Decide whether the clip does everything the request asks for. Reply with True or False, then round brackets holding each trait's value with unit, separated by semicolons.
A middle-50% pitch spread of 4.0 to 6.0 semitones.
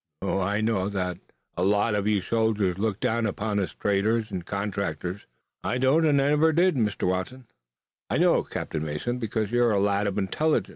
False (3.1 semitones)